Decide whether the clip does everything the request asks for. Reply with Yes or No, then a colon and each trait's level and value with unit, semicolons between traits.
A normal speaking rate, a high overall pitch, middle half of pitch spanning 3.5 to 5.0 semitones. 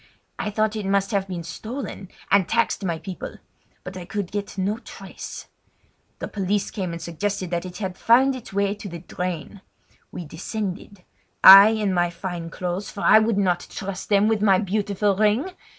No: average, 180 wpm; high, 195 Hz; narrow, 2.5 semitones